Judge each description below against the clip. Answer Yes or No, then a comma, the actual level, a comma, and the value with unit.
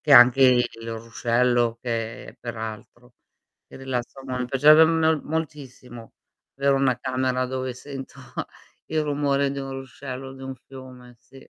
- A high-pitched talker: No, low, 130 Hz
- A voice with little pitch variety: Yes, narrow, 2.1 semitones